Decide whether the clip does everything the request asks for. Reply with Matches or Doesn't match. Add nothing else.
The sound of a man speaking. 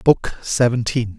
Matches